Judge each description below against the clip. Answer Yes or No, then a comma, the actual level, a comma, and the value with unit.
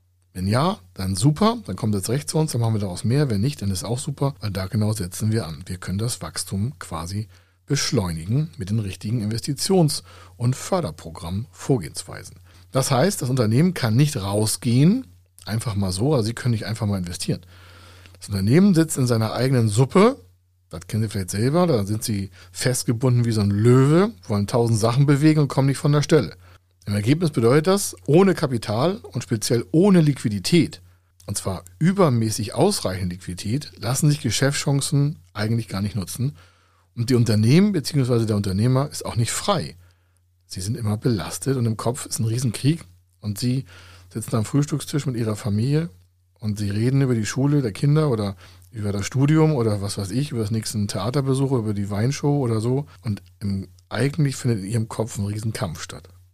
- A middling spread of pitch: No, wide, 5.9 semitones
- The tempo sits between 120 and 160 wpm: No, average, 185 wpm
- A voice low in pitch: Yes, low, 115 Hz